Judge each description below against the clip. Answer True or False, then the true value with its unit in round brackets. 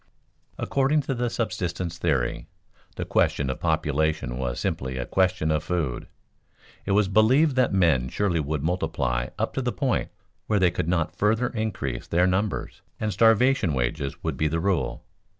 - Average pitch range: False (6.6 semitones)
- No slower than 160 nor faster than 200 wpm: True (165 wpm)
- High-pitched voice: False (90 Hz)